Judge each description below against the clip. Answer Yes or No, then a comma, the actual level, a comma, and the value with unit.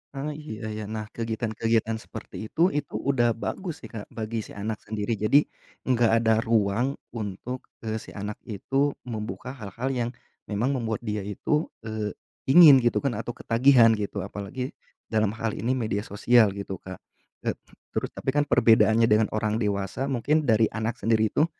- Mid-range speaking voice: No, low, 115 Hz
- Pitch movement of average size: Yes, average, 3.0 semitones